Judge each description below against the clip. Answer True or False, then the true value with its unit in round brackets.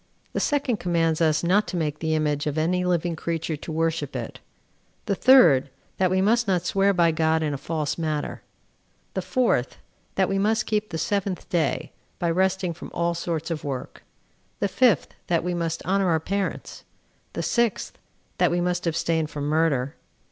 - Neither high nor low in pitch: True (170 Hz)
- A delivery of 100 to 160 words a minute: False (180 wpm)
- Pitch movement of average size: True (3.3 semitones)